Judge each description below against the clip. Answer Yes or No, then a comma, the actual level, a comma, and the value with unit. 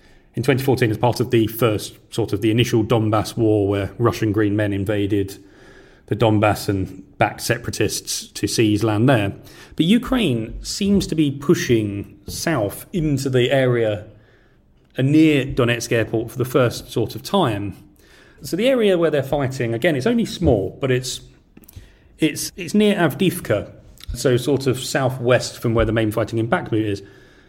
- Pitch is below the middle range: Yes, low, 120 Hz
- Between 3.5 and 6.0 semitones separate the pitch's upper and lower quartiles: Yes, average, 4.4 semitones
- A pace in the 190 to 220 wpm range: No, average, 160 wpm